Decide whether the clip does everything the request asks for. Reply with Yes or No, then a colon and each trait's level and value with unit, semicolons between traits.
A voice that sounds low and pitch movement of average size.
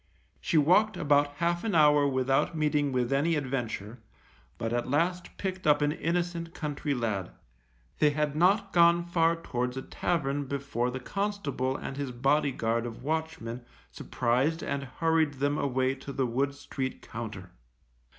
No: medium, 145 Hz; average, 4.2 semitones